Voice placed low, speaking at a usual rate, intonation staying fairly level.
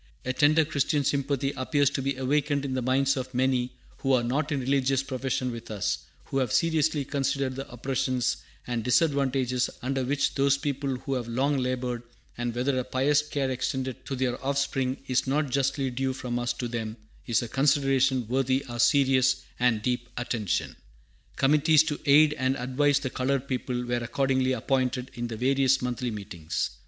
Yes: low, 130 Hz; average, 175 wpm; narrow, 1.9 semitones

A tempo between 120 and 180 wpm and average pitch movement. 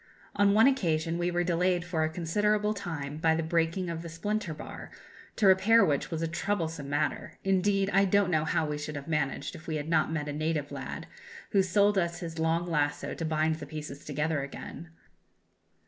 No: average, 200 wpm; average, 3.3 semitones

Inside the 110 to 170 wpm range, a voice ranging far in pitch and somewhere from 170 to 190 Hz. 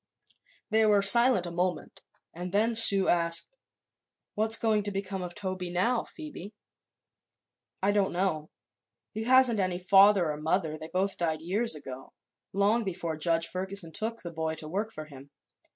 No: average, 160 wpm; average, 3.8 semitones; medium, 185 Hz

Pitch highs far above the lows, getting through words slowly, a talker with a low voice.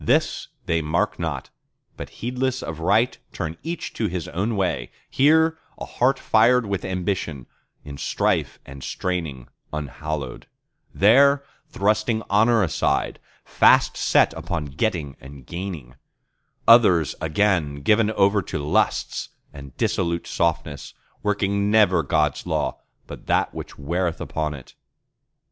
Yes: wide, 6.1 semitones; slow, 125 wpm; very low, 90 Hz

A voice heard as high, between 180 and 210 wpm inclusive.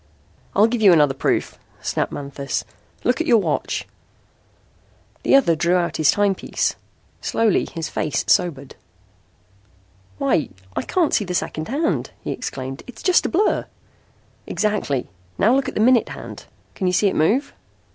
No: high, 195 Hz; average, 155 wpm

